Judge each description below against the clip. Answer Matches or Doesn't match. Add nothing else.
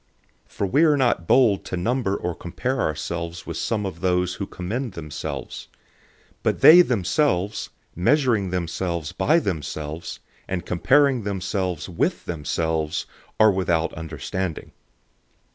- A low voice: Matches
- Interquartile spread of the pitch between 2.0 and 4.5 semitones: Doesn't match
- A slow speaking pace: Matches